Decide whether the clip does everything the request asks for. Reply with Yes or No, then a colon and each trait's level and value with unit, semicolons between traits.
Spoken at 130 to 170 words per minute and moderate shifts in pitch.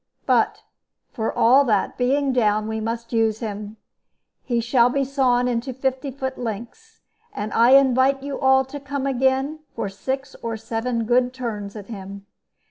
Yes: average, 160 wpm; average, 3.1 semitones